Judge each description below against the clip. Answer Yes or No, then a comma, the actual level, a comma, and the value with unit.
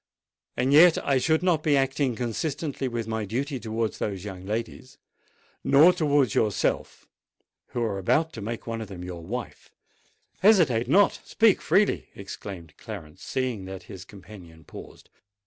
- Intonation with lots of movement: Yes, wide, 6.3 semitones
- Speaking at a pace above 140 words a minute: Yes, average, 150 wpm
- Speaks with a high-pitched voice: No, low, 115 Hz